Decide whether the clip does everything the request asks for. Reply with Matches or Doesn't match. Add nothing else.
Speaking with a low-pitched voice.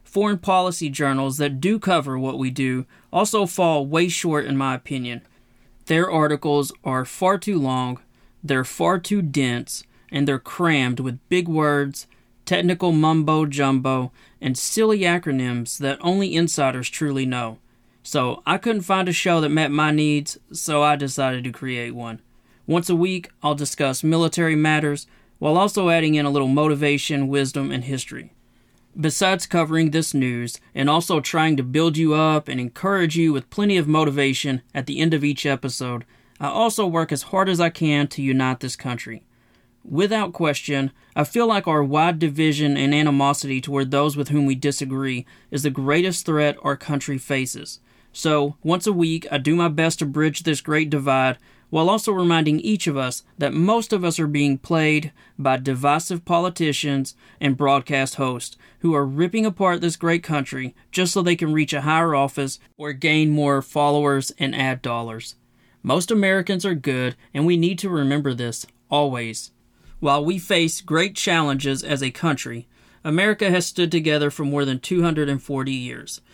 Doesn't match